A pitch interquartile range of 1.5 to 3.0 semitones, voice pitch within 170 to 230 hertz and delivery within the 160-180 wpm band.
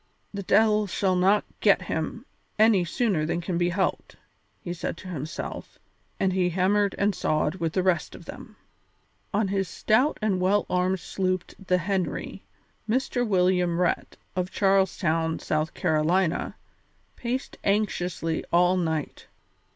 No: narrow, 2.6 semitones; medium, 185 Hz; average, 145 wpm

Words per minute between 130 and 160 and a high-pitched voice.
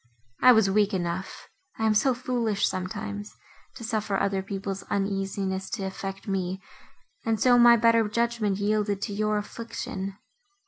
Yes: slow, 135 wpm; high, 205 Hz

